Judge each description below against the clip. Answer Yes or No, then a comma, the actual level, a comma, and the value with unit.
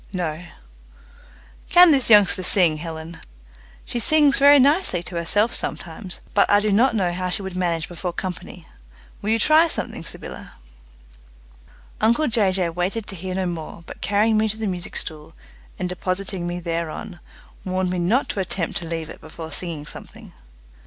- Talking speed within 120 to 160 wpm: No, average, 170 wpm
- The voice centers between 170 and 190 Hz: Yes, medium, 185 Hz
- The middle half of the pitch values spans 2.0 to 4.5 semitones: Yes, average, 4.0 semitones